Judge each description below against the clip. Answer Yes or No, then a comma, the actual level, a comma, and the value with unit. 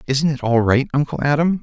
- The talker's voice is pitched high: No, medium, 140 Hz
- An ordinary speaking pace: No, fast, 220 wpm